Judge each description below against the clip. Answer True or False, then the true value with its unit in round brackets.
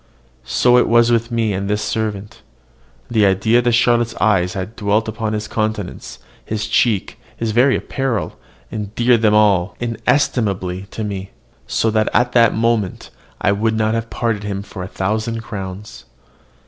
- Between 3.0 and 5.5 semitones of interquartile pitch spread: False (2.5 semitones)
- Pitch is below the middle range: True (110 Hz)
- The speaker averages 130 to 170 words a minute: True (160 wpm)